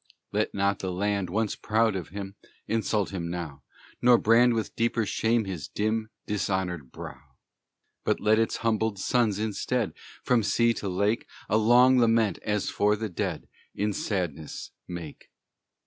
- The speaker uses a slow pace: No, average, 150 wpm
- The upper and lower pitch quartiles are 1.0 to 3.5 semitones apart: Yes, average, 3.0 semitones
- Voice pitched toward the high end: No, low, 105 Hz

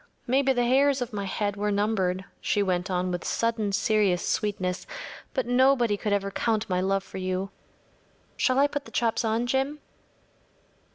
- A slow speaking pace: No, average, 170 wpm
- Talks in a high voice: Yes, high, 210 Hz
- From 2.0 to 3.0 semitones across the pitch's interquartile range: No, average, 4.1 semitones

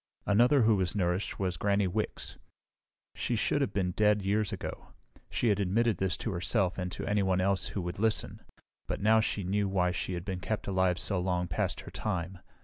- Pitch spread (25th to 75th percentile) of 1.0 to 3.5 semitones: Yes, narrow, 2.5 semitones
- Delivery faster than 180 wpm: Yes, average, 200 wpm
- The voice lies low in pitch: Yes, very low, 95 Hz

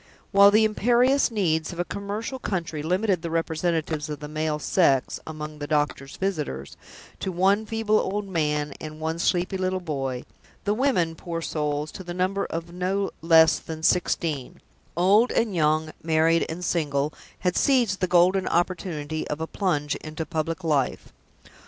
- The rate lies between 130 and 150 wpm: No, average, 160 wpm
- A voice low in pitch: No, medium, 165 Hz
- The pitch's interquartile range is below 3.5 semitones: No, average, 3.8 semitones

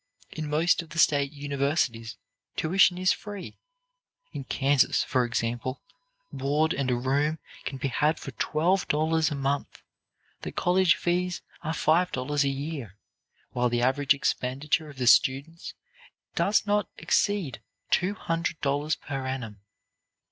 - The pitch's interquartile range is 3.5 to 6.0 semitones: Yes, average, 3.9 semitones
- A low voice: No, medium, 145 Hz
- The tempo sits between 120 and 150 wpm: Yes, average, 140 wpm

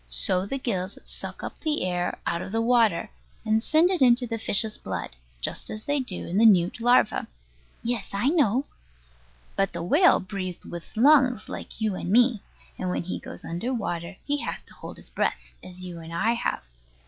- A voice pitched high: Yes, high, 215 Hz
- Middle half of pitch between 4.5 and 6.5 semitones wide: Yes, average, 5.3 semitones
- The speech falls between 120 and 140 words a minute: No, average, 195 wpm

